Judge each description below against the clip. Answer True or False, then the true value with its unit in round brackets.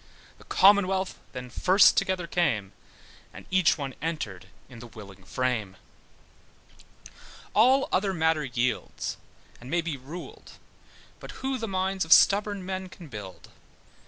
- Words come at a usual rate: False (130 wpm)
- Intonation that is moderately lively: False (7.2 semitones)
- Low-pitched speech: False (165 Hz)